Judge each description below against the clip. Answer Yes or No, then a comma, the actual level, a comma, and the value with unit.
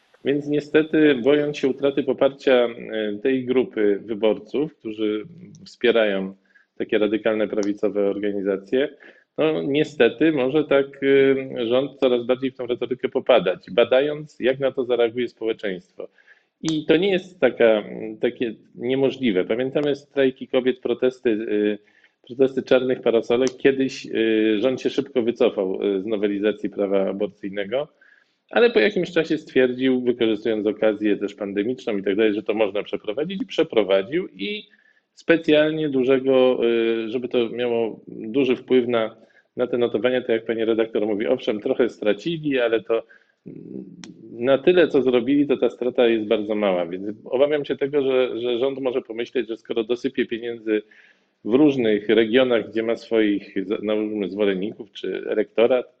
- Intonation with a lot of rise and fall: No, average, 3.7 semitones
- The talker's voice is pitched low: Yes, low, 125 Hz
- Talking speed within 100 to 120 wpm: No, average, 135 wpm